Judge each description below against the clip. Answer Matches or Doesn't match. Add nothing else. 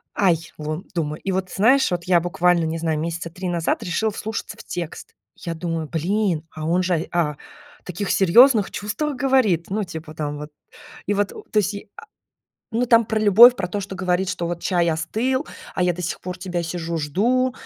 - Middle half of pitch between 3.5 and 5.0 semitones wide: Matches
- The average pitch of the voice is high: Doesn't match